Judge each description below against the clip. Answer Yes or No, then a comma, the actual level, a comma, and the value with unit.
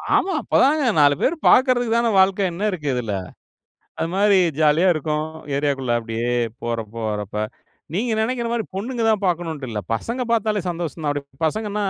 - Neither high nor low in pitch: Yes, medium, 175 Hz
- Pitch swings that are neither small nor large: No, wide, 7.9 semitones